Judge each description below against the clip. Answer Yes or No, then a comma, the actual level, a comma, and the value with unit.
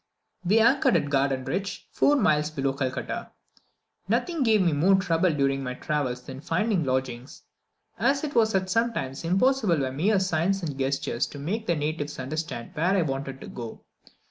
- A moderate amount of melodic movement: No, wide, 6.3 semitones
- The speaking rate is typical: Yes, average, 165 wpm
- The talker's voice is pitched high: No, medium, 155 Hz